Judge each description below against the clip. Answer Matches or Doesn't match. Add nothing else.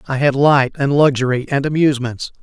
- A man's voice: Matches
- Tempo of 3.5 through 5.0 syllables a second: Doesn't match